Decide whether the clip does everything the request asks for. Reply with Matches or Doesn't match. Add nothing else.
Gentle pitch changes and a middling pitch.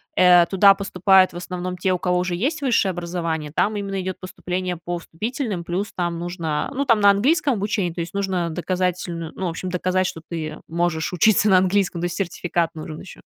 Matches